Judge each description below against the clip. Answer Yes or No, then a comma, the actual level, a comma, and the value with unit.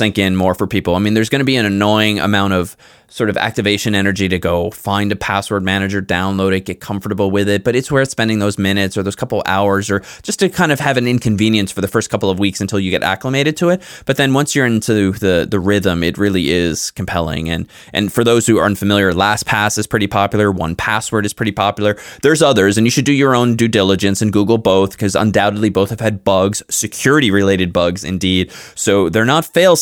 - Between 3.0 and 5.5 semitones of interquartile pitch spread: No, narrow, 2.5 semitones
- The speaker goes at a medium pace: No, fast, 230 wpm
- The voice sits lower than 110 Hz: Yes, low, 100 Hz